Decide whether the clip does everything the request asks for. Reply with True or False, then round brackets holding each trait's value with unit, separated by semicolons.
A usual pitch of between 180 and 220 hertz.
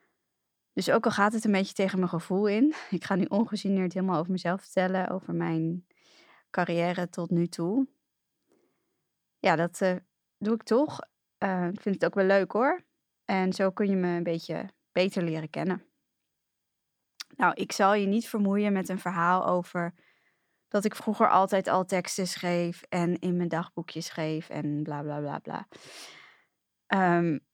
True (185 Hz)